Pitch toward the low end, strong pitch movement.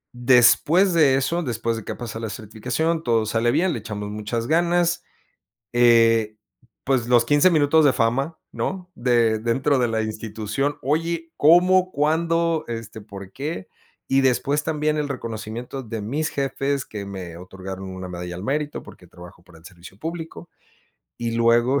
Yes: low, 120 Hz; wide, 5.7 semitones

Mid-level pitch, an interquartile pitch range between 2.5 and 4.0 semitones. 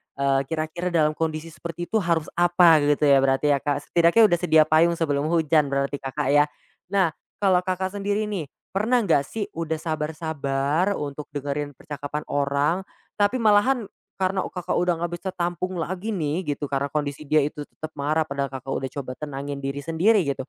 Yes: medium, 155 Hz; average, 3.7 semitones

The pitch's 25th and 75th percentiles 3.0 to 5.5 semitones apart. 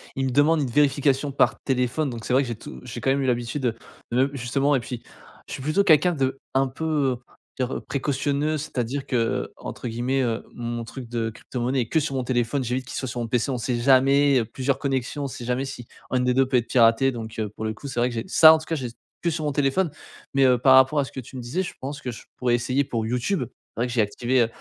No: narrow, 2.6 semitones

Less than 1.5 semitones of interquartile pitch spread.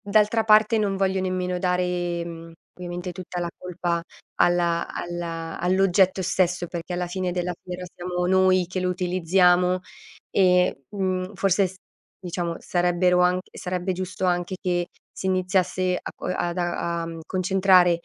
Yes: narrow, 1.1 semitones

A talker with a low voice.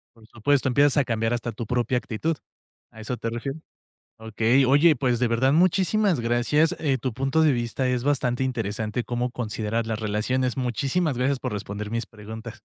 Yes: low, 125 Hz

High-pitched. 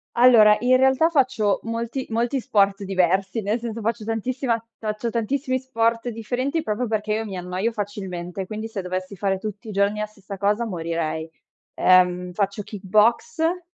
Yes: high, 215 Hz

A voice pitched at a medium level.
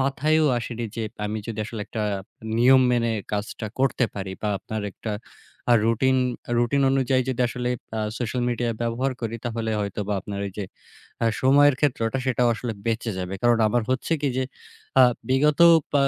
No: low, 120 Hz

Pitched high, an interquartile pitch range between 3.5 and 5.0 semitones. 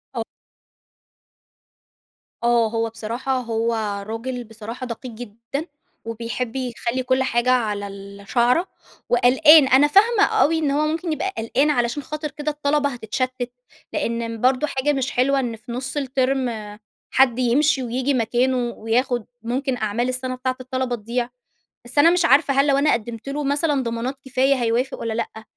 No: very high, 255 Hz; average, 2.9 semitones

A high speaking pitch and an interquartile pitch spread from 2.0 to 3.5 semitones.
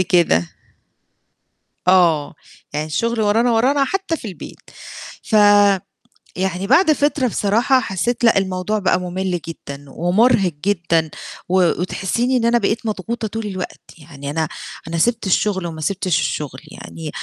No: high, 195 Hz; average, 5.2 semitones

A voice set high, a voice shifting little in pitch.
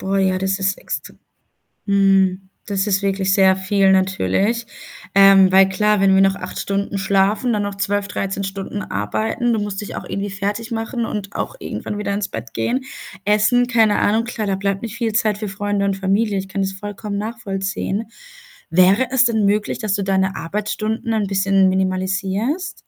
Yes: high, 200 Hz; narrow, 1.7 semitones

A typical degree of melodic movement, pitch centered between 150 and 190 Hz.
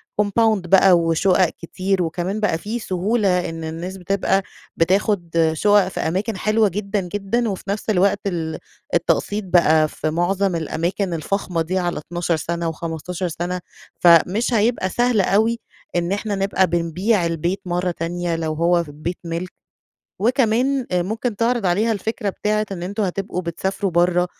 Yes: average, 3.2 semitones; medium, 185 Hz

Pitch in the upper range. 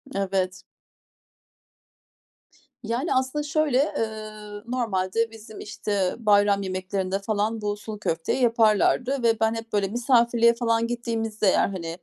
Yes: high, 220 Hz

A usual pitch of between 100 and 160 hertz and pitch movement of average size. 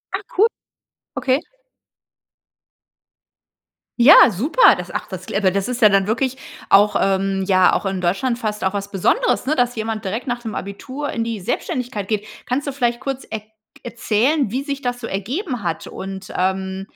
No: high, 220 Hz; average, 4.8 semitones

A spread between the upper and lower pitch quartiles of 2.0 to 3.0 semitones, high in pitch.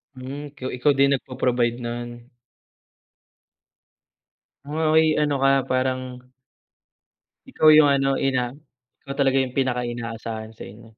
No: narrow, 2.4 semitones; low, 130 Hz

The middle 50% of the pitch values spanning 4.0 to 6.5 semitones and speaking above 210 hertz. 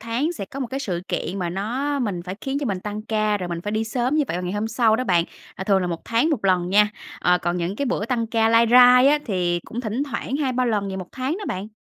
Yes: average, 5.1 semitones; high, 220 Hz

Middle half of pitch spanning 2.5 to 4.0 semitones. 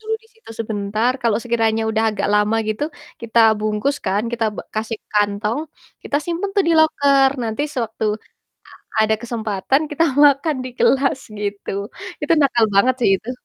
No: average, 4.5 semitones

